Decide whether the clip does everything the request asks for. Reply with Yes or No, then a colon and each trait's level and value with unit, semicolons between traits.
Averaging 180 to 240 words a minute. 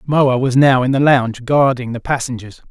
Yes: average, 200 wpm